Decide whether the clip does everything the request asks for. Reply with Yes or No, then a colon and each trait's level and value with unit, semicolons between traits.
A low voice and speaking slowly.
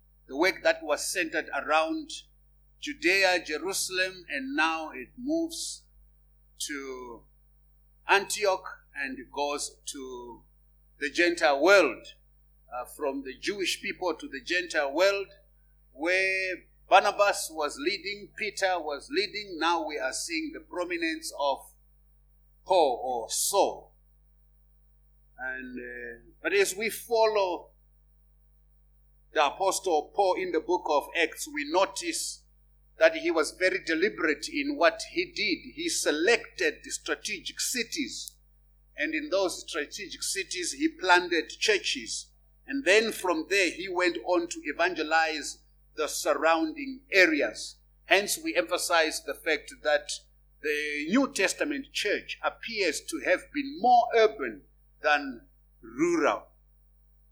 No: medium, 175 Hz; slow, 120 wpm